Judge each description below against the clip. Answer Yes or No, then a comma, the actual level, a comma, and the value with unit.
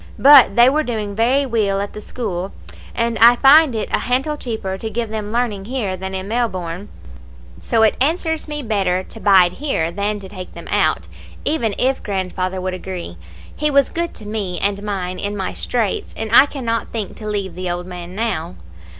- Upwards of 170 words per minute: Yes, average, 195 wpm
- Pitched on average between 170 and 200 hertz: No, high, 210 Hz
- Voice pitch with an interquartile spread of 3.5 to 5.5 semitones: Yes, average, 4.3 semitones